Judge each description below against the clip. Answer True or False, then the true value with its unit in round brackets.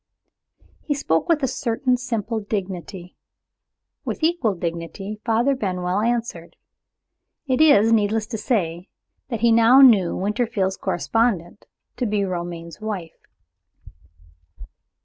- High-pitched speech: True (215 Hz)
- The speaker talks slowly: True (110 wpm)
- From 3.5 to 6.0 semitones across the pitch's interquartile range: True (4.7 semitones)